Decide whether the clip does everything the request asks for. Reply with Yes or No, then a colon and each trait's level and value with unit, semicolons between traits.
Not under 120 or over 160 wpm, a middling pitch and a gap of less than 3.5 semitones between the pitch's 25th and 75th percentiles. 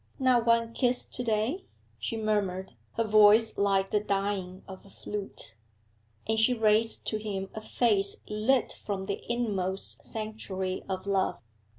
No: average, 150 wpm; high, 210 Hz; narrow, 2.6 semitones